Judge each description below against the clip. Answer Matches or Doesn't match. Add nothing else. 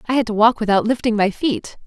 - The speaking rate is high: Matches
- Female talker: Matches